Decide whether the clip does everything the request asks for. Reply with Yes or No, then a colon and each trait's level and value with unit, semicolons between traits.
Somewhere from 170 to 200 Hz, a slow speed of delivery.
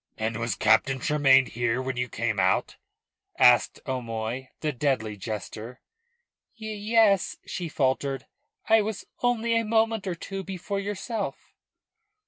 No: medium, 140 Hz; slow, 130 wpm